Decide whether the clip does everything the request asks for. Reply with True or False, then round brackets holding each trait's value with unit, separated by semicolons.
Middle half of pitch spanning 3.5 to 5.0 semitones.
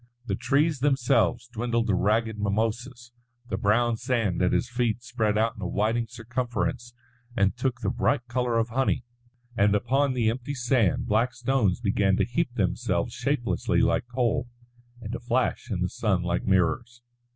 False (2.8 semitones)